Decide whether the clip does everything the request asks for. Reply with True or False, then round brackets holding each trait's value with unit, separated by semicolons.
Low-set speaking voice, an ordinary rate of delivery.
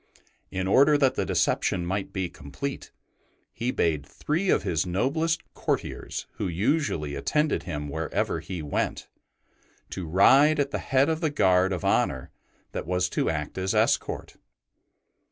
True (95 Hz; 150 wpm)